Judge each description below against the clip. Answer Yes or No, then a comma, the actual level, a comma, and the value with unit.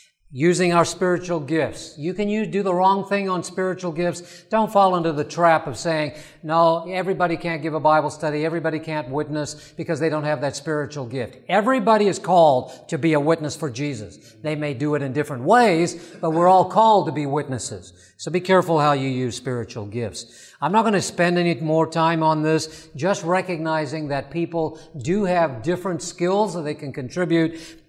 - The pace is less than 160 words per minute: No, average, 195 wpm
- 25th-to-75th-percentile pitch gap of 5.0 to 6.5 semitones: No, average, 2.9 semitones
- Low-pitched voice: No, medium, 160 Hz